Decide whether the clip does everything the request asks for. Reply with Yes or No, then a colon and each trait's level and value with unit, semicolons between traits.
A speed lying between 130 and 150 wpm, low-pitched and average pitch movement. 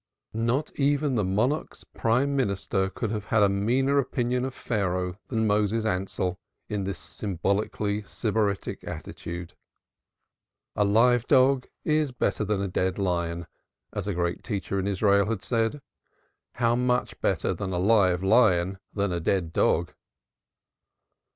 Yes: average, 140 wpm; low, 105 Hz; average, 4.1 semitones